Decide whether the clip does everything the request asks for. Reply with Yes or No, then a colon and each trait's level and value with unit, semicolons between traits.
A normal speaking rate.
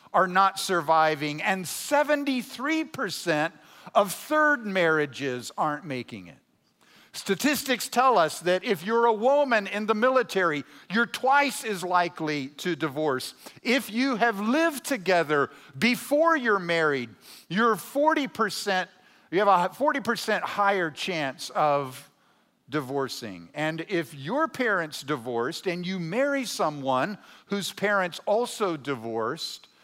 No: slow, 120 wpm